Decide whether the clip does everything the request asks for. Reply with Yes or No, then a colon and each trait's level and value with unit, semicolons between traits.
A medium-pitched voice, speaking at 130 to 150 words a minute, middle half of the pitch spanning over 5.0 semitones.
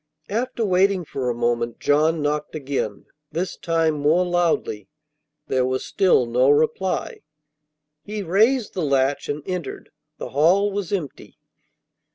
Yes: medium, 160 Hz; slow, 135 wpm; wide, 5.5 semitones